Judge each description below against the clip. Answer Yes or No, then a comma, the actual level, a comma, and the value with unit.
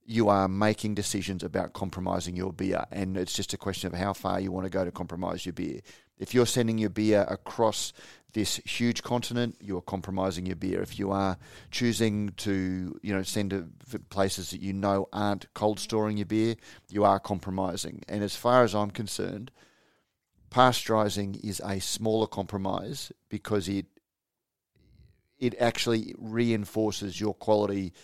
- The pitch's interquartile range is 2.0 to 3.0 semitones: Yes, narrow, 2.4 semitones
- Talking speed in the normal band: Yes, average, 165 wpm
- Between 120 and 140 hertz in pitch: No, low, 100 Hz